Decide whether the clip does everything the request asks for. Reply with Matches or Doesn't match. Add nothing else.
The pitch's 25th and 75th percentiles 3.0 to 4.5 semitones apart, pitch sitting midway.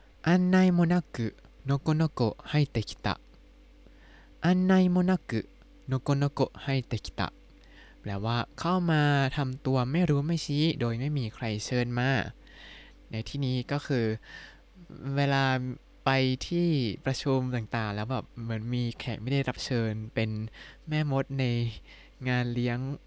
Doesn't match